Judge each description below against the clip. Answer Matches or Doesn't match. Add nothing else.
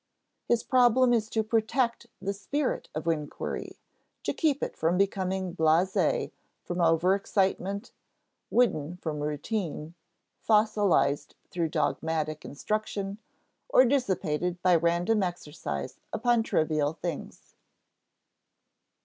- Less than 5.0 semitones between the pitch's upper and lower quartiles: Doesn't match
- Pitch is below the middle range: Doesn't match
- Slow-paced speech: Matches